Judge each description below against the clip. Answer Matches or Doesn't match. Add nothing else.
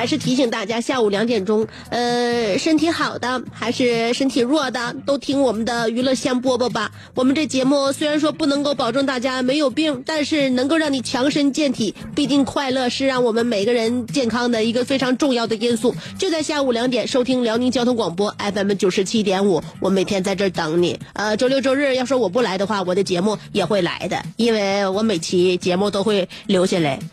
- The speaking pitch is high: Matches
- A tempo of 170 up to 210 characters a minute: Doesn't match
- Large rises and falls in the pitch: Doesn't match